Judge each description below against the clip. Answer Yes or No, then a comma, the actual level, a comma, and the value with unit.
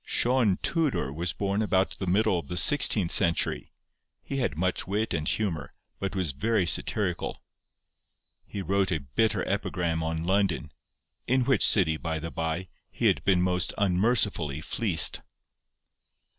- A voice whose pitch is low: Yes, very low, 95 Hz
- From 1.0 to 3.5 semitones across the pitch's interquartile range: No, average, 4.3 semitones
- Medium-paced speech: Yes, average, 145 wpm